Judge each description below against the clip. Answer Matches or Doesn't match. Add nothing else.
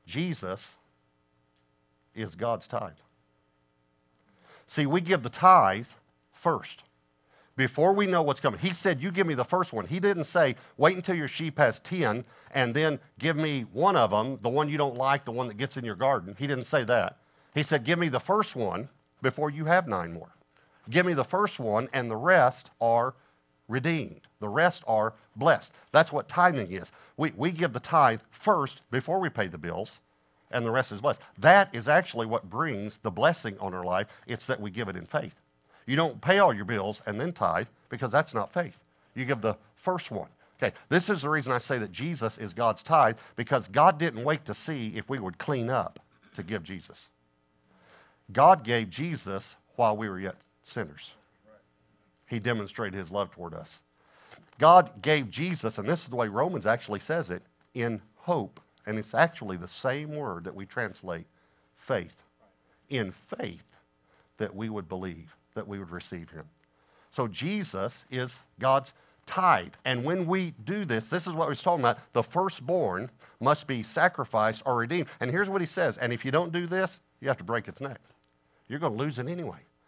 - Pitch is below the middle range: Matches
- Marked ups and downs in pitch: Matches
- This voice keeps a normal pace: Matches